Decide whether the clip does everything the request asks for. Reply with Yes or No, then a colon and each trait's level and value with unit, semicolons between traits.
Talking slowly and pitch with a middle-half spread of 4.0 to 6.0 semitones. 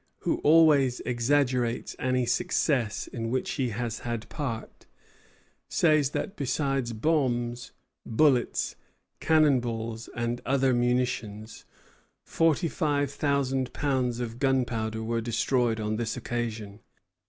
No: slow, 115 wpm; average, 3.2 semitones